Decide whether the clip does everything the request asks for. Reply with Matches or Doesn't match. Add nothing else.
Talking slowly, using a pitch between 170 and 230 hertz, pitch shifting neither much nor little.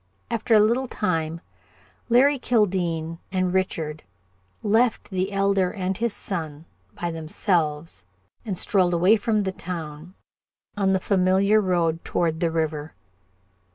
Matches